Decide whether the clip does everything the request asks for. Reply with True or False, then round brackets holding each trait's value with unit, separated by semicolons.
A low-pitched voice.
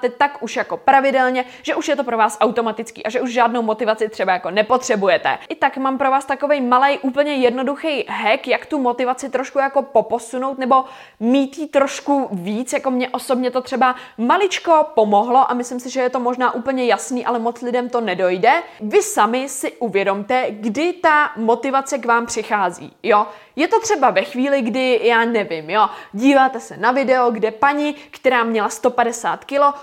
False (255 Hz)